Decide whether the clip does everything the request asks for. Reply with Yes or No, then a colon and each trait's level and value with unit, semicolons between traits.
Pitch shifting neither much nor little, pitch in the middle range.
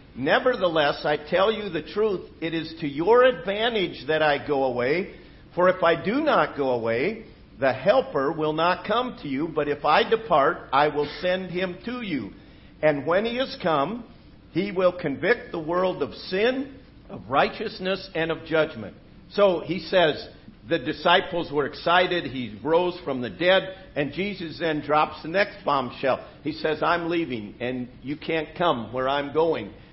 Yes: average, 4.0 semitones; medium, 165 Hz